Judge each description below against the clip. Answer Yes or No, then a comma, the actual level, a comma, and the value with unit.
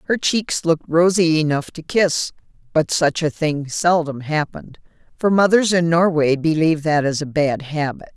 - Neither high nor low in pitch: Yes, medium, 160 Hz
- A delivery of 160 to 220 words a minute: Yes, average, 170 wpm